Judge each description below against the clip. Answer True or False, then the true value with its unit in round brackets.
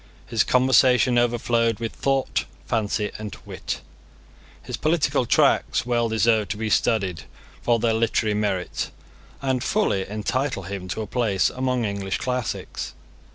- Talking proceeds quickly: False (135 wpm)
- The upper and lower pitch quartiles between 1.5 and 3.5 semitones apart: True (3.2 semitones)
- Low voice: True (115 Hz)